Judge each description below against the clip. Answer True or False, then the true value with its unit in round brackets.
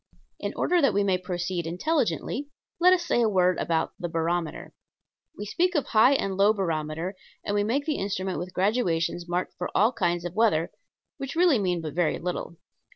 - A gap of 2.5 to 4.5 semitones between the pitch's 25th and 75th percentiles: False (5.2 semitones)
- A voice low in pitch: False (190 Hz)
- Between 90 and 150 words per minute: False (190 wpm)